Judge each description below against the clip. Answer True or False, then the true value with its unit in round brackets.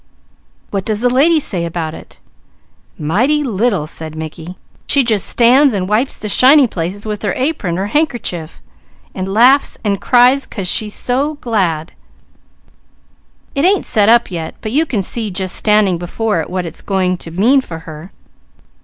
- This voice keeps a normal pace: True (165 wpm)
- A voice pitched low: False (210 Hz)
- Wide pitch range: True (5.9 semitones)